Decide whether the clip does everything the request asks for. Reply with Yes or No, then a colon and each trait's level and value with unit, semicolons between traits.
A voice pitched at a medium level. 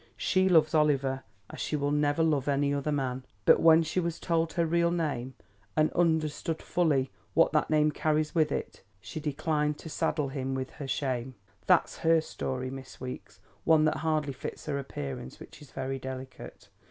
Yes: medium, 150 Hz